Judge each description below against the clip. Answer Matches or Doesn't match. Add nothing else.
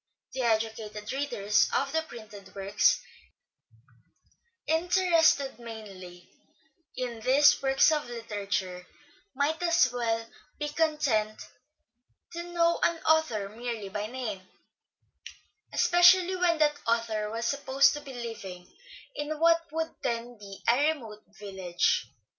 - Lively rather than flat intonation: Matches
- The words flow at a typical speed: Doesn't match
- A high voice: Matches